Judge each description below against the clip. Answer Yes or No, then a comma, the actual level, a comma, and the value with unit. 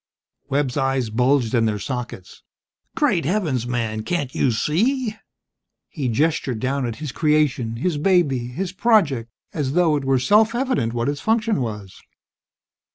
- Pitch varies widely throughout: Yes, wide, 6.5 semitones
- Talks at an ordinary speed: Yes, average, 150 wpm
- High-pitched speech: No, medium, 140 Hz